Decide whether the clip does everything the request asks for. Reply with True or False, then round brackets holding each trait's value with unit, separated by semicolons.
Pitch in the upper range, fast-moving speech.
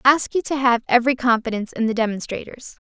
True (245 Hz; 210 wpm)